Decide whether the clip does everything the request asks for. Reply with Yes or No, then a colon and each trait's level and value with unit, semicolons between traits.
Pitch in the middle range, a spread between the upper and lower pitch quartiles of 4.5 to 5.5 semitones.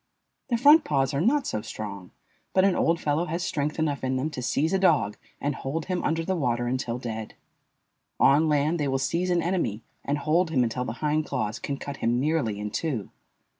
Yes: medium, 145 Hz; average, 5.0 semitones